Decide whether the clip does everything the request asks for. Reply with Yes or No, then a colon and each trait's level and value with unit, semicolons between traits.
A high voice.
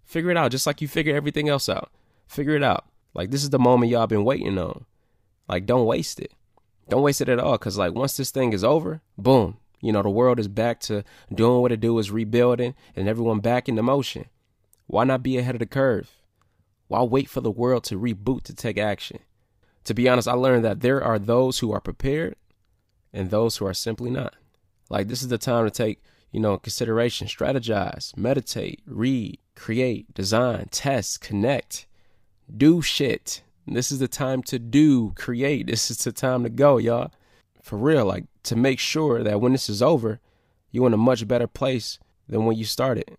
No: low, 120 Hz